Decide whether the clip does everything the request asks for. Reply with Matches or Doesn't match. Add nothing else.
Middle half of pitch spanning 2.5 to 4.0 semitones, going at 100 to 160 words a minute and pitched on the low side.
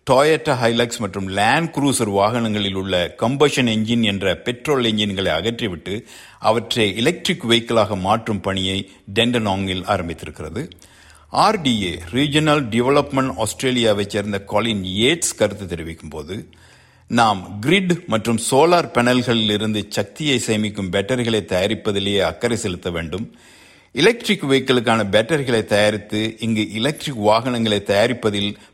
Matches